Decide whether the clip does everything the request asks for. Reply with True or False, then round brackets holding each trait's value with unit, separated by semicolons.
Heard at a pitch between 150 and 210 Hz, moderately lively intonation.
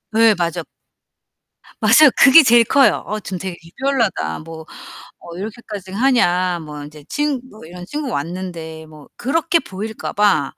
False (190 Hz; 6.5 semitones)